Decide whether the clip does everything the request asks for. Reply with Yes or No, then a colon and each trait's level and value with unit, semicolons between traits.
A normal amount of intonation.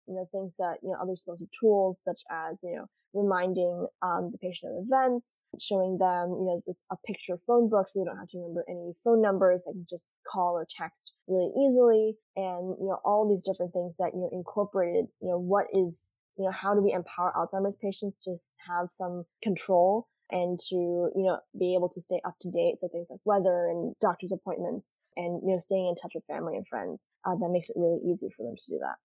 No: narrow, 1.9 semitones